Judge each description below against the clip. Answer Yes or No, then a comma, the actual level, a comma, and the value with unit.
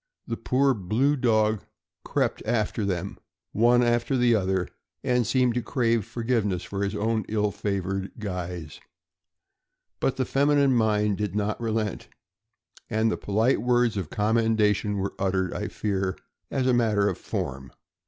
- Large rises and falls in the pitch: No, average, 3.3 semitones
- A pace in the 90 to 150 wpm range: Yes, average, 145 wpm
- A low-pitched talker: Yes, low, 110 Hz